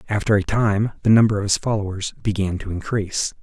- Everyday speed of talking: Yes, average, 190 wpm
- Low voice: Yes, low, 100 Hz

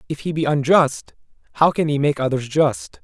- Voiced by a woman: No, male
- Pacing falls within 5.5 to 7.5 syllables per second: No, 5.0 syllables/s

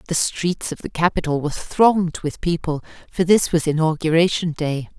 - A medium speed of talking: Yes, average, 170 wpm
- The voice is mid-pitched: Yes, medium, 165 Hz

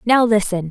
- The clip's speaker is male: No, female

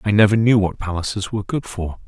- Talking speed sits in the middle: No, fast, 230 wpm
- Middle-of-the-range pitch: No, low, 100 Hz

